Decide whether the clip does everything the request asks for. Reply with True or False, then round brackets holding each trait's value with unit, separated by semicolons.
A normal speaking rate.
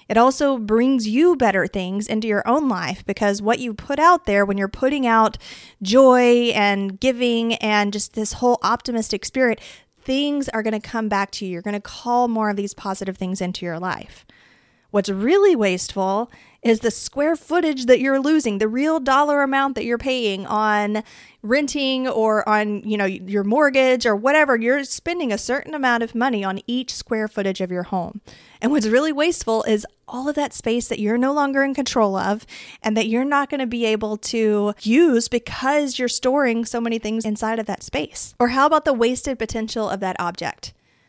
True (195 wpm)